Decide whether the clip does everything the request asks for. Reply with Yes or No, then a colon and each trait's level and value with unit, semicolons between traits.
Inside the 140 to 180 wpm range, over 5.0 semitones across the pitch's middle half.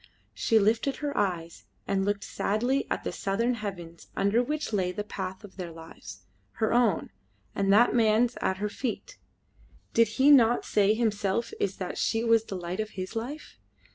No: average, 175 wpm; average, 3.5 semitones